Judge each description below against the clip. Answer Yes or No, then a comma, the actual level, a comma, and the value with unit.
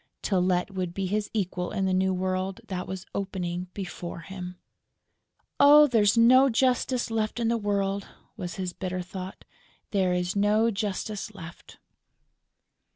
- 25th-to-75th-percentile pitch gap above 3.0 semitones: No, average, 2.7 semitones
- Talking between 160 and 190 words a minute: No, average, 145 wpm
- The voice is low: No, high, 195 Hz